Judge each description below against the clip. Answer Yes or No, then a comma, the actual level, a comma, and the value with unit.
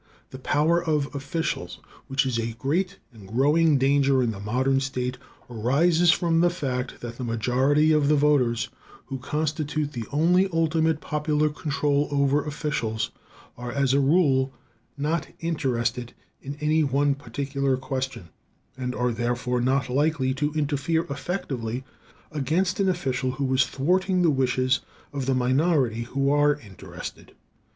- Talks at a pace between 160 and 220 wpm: No, average, 145 wpm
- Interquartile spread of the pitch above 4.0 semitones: No, average, 3.3 semitones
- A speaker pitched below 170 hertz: Yes, medium, 140 Hz